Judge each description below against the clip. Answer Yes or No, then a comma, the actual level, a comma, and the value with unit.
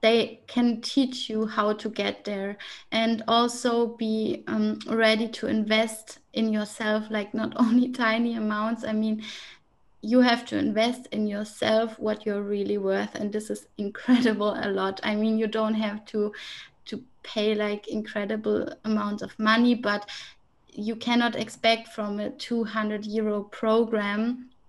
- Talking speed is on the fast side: No, average, 150 wpm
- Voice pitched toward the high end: Yes, high, 220 Hz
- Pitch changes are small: Yes, narrow, 1.5 semitones